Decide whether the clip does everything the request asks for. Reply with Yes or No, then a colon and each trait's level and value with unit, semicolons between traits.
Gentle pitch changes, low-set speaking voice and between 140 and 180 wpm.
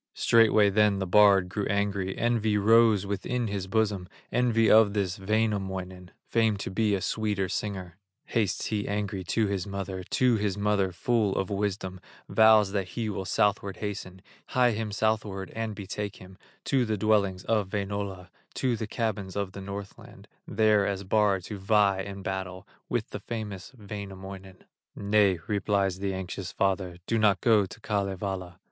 Yes: narrow, 2.0 semitones; low, 100 Hz; average, 160 wpm